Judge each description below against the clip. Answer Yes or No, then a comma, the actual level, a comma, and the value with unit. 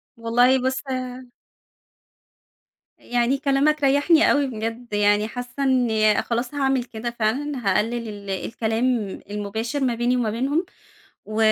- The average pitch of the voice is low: No, high, 240 Hz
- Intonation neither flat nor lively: Yes, average, 3.4 semitones